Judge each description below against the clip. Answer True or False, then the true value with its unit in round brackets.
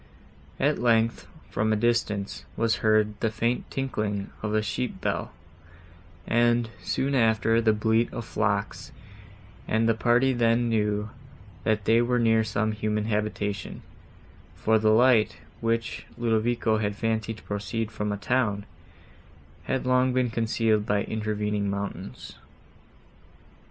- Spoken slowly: True (130 wpm)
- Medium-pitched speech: False (110 Hz)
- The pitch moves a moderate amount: False (1.8 semitones)